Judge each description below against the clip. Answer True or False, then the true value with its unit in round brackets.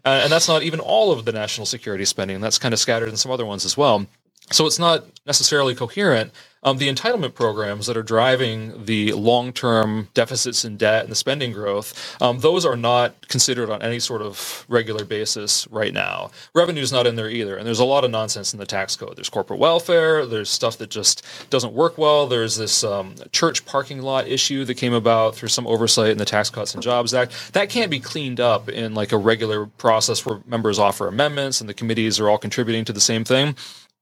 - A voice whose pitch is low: True (115 Hz)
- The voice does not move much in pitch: False (3.5 semitones)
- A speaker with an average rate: False (220 wpm)